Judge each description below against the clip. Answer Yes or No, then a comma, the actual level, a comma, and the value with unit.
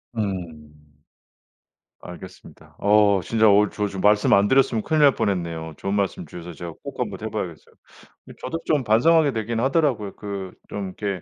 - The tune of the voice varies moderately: Yes, average, 3.6 semitones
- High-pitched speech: No, low, 105 Hz